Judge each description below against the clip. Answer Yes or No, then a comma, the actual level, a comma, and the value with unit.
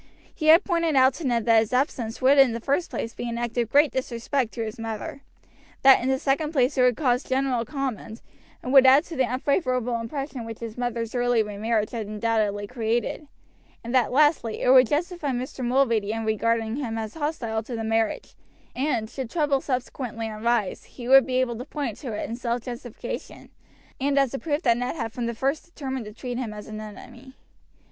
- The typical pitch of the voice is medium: No, high, 245 Hz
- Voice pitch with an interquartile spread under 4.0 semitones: Yes, average, 3.1 semitones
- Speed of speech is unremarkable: No, fast, 210 wpm